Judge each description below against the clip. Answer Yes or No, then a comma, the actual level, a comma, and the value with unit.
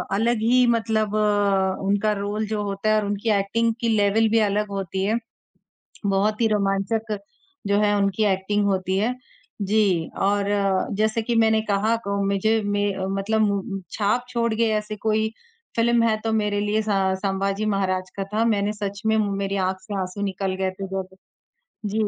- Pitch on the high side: Yes, high, 205 Hz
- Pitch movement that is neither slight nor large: No, narrow, 1.8 semitones